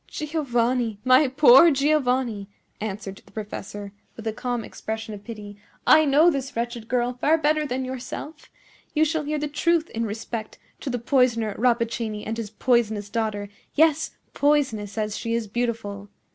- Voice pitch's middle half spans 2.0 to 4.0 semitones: No, average, 4.5 semitones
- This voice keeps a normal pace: Yes, average, 160 wpm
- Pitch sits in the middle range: No, high, 240 Hz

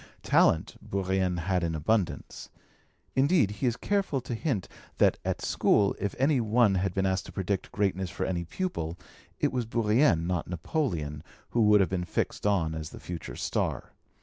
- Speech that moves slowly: No, average, 175 wpm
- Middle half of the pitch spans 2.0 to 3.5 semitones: No, average, 5.0 semitones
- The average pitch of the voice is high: No, very low, 95 Hz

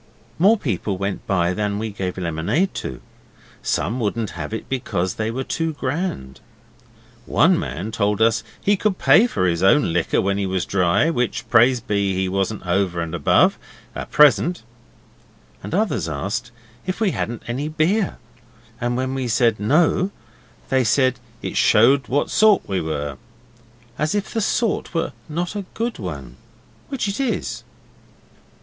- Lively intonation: Yes, wide, 8.7 semitones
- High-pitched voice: No, low, 115 Hz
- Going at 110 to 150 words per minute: No, average, 160 wpm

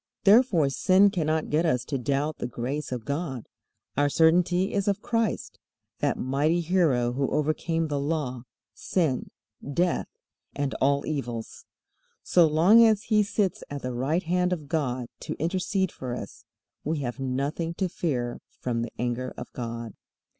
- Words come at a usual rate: Yes, average, 155 wpm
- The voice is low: No, medium, 150 Hz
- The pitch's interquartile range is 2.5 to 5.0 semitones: No, wide, 5.6 semitones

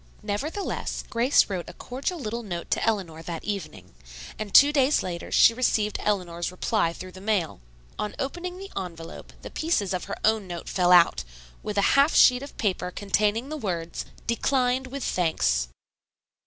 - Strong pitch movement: Yes, wide, 6.2 semitones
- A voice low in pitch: No, high, 210 Hz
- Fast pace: No, average, 170 wpm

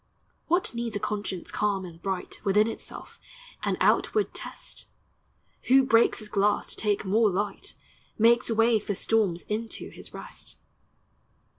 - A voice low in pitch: No, high, 210 Hz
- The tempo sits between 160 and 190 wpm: No, average, 140 wpm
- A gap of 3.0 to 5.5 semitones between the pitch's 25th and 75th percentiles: No, narrow, 2.4 semitones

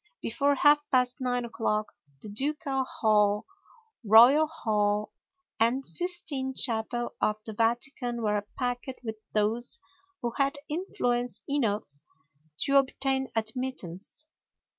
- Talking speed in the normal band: No, slow, 110 wpm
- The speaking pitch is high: Yes, high, 245 Hz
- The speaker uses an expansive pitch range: No, average, 3.8 semitones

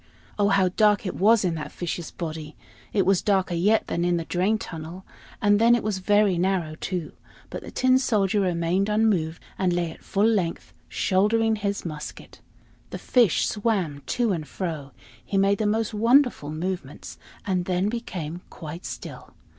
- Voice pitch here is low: No, high, 190 Hz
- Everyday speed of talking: Yes, average, 170 wpm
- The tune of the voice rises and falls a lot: No, average, 3.8 semitones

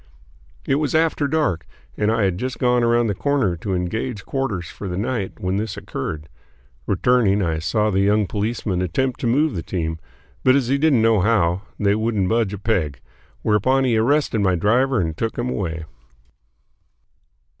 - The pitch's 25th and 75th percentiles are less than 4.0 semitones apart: No, average, 5.1 semitones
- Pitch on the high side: No, low, 110 Hz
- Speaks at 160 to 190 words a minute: Yes, average, 175 wpm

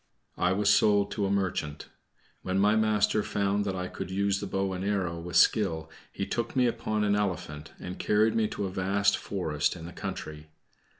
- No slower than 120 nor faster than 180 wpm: No, average, 195 wpm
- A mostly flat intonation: Yes, narrow, 2.3 semitones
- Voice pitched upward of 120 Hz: No, low, 100 Hz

